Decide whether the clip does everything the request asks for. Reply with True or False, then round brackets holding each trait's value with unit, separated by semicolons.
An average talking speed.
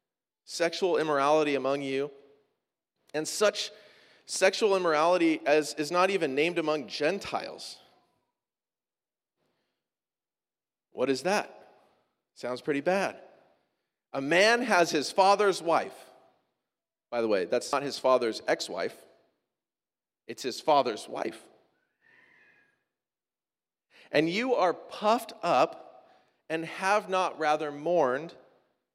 False (105 wpm)